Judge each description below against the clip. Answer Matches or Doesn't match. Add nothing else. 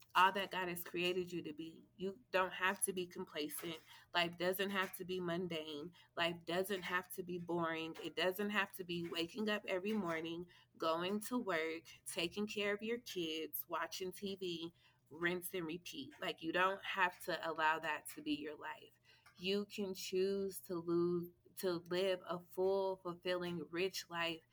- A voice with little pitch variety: Matches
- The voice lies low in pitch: Doesn't match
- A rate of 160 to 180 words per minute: Matches